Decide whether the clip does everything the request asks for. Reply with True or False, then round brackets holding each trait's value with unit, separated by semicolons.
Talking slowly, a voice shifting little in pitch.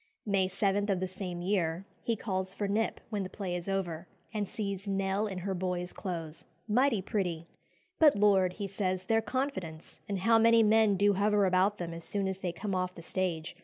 False (200 wpm; 2.3 semitones)